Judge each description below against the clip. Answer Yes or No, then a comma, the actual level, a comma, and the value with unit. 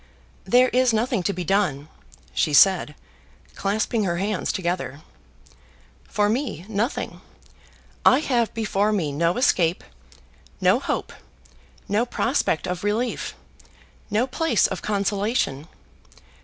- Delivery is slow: Yes, slow, 115 wpm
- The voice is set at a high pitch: Yes, high, 205 Hz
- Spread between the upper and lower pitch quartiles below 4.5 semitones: No, average, 4.8 semitones